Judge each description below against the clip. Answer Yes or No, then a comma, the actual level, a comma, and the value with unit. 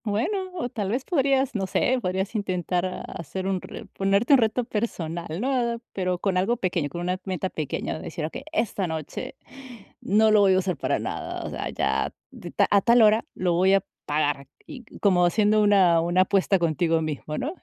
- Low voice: No, high, 190 Hz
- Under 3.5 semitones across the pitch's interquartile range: No, average, 4.2 semitones